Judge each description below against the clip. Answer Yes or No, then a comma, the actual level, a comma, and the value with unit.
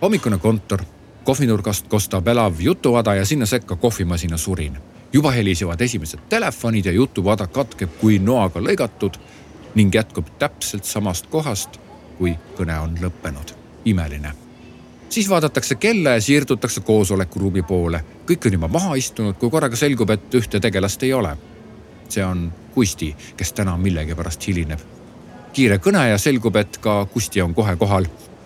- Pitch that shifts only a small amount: No, average, 4.8 semitones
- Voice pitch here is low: Yes, low, 105 Hz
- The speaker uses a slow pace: No, average, 145 wpm